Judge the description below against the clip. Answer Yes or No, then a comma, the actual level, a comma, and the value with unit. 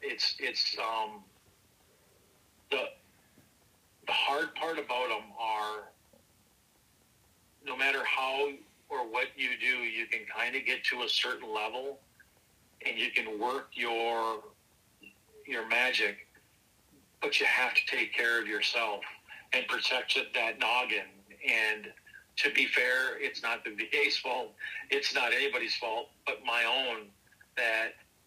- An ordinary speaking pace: No, slow, 130 wpm